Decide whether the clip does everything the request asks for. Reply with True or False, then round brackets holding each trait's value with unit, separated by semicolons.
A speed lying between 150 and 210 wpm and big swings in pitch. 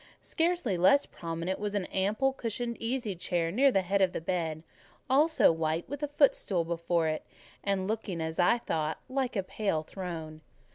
True (175 wpm; 6.2 semitones)